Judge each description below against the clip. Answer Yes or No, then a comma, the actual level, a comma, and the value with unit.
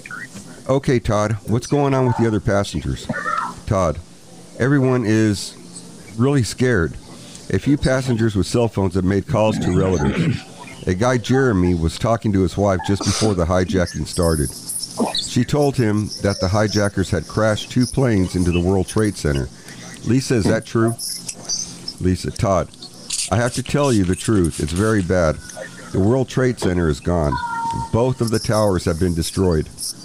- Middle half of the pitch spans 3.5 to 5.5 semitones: Yes, average, 5.2 semitones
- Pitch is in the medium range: No, low, 105 Hz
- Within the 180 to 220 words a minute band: No, average, 165 wpm